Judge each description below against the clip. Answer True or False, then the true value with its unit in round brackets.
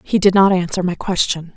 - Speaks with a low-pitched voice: False (185 Hz)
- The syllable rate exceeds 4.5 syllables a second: True (5.5 syllables/s)